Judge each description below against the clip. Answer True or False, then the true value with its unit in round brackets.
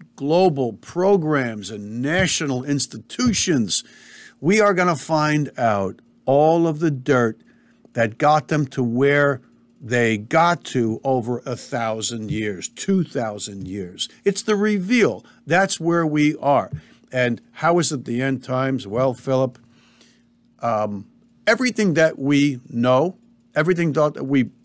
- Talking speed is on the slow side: True (130 wpm)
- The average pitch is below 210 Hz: True (140 Hz)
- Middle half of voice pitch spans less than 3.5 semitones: False (5.5 semitones)